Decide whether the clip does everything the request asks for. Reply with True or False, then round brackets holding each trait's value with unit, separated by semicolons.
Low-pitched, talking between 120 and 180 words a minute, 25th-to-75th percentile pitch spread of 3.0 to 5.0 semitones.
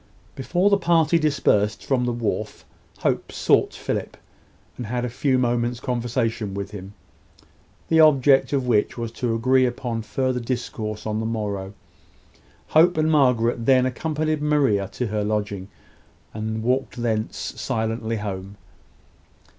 True (120 Hz; 140 wpm; 3.7 semitones)